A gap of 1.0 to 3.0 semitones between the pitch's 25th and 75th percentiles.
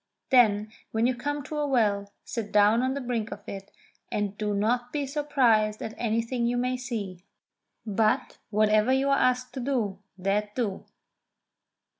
No: average, 3.4 semitones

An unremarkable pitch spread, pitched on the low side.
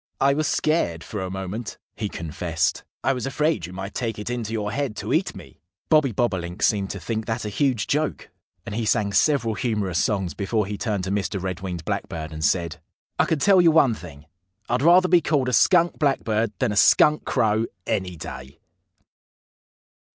No: wide, 6.2 semitones; low, 105 Hz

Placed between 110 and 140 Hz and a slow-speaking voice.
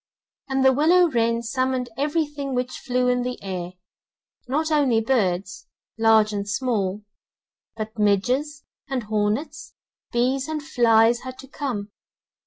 No: very high, 250 Hz; slow, 130 wpm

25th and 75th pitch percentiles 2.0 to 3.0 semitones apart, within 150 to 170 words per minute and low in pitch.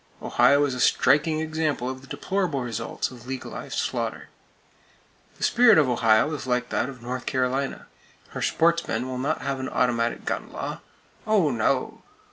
No: average, 3.8 semitones; average, 160 wpm; low, 130 Hz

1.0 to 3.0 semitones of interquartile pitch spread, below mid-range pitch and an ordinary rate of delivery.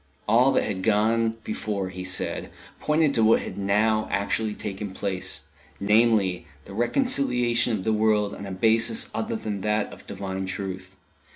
Yes: narrow, 2.5 semitones; low, 105 Hz; average, 160 wpm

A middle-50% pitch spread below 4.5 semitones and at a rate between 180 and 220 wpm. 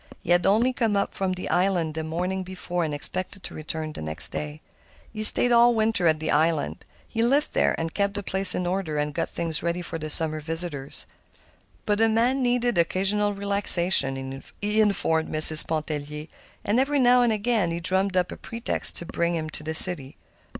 No: average, 4.8 semitones; average, 195 wpm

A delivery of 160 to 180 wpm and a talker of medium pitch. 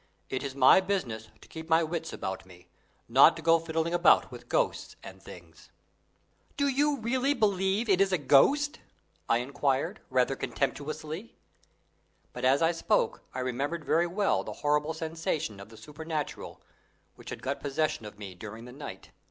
Yes: average, 170 wpm; medium, 155 Hz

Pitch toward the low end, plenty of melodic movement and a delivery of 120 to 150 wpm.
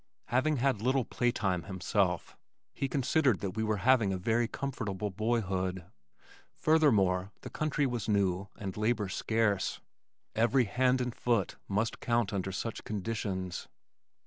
No: low, 110 Hz; average, 4.2 semitones; average, 140 wpm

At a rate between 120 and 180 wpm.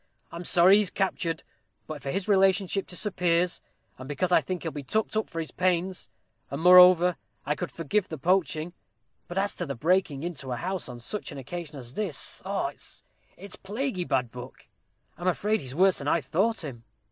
No: average, 195 wpm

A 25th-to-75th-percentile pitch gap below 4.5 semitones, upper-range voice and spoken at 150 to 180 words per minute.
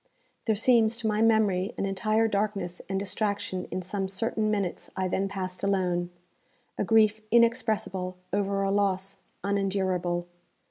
No: narrow, 2.4 semitones; high, 200 Hz; average, 140 wpm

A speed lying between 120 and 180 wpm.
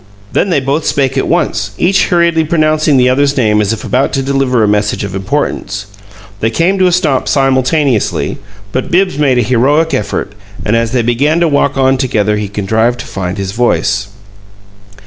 No: average, 190 wpm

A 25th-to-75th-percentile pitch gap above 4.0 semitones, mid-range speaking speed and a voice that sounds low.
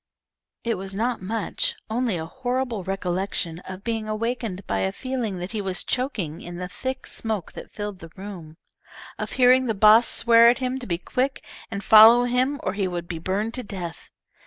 No: average, 4.8 semitones; average, 190 wpm; high, 215 Hz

